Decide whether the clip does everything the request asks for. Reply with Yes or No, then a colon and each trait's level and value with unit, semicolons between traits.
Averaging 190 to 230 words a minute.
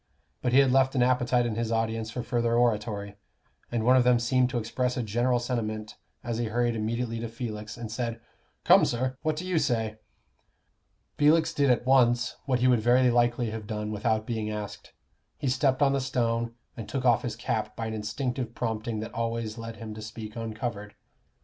Yes: average, 200 wpm